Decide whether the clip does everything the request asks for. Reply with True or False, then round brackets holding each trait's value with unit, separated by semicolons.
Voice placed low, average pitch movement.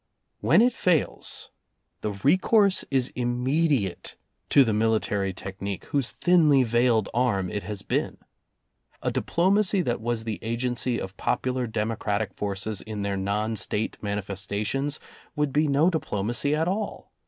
False (120 Hz; 5.8 semitones)